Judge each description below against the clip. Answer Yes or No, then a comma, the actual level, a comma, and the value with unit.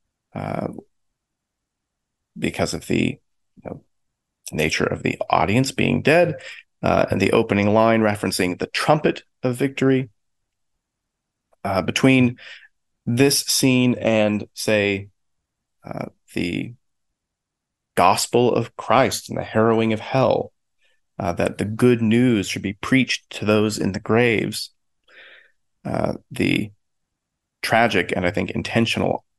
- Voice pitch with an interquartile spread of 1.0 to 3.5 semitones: No, average, 3.9 semitones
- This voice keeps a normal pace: No, slow, 120 wpm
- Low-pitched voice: Yes, low, 110 Hz